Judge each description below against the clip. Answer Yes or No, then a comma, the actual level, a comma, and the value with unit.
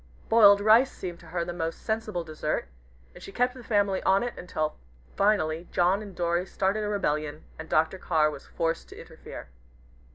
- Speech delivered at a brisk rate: No, average, 185 wpm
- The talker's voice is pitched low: No, medium, 180 Hz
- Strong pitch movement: No, average, 4.2 semitones